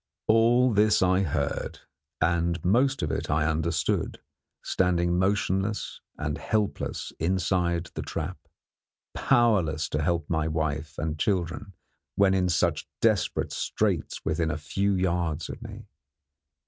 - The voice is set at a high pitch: No, very low, 90 Hz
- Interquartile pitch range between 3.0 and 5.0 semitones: Yes, average, 3.9 semitones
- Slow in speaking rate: Yes, slow, 125 wpm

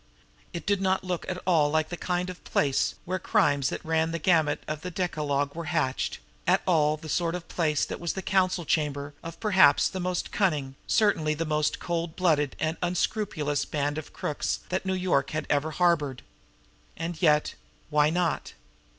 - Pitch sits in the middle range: Yes, medium, 165 Hz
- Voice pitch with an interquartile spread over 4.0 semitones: No, average, 3.2 semitones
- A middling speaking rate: Yes, average, 180 wpm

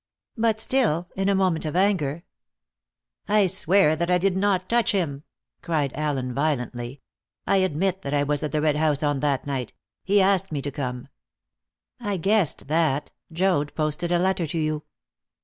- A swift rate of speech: No, average, 175 wpm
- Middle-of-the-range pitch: Yes, medium, 160 Hz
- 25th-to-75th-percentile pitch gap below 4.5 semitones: No, average, 4.8 semitones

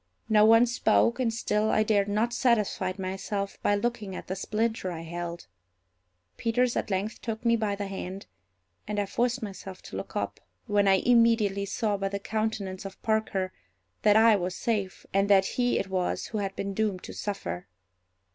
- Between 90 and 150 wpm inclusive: No, average, 185 wpm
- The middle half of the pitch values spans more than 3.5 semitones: No, narrow, 2.6 semitones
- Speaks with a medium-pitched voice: No, high, 205 Hz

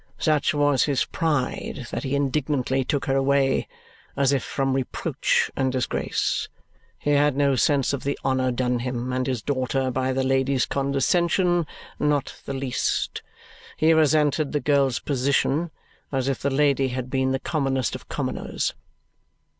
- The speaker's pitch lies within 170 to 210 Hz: No, low, 135 Hz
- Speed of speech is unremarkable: Yes, average, 155 wpm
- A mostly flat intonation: Yes, narrow, 1.8 semitones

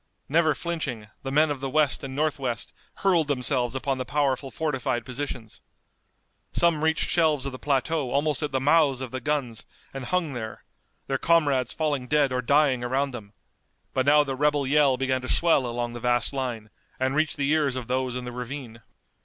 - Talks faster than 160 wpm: Yes, average, 190 wpm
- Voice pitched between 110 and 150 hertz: Yes, low, 135 Hz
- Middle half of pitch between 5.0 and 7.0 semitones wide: No, average, 2.9 semitones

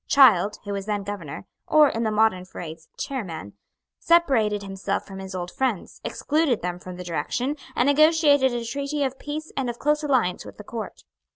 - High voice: Yes, high, 225 Hz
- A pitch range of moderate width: No, wide, 6.7 semitones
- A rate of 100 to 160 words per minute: No, average, 185 wpm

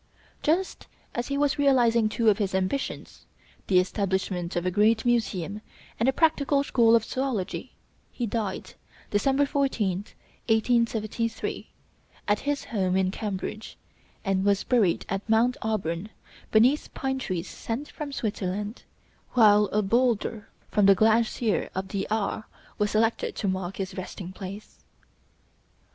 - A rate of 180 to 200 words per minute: No, slow, 135 wpm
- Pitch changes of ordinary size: Yes, average, 3.8 semitones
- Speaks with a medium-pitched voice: No, high, 215 Hz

